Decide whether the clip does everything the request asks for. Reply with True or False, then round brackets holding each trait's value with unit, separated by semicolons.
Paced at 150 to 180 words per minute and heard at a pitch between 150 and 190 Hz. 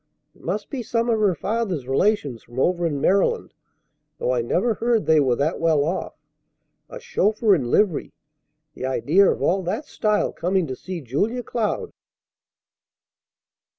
True (155 wpm; 185 Hz)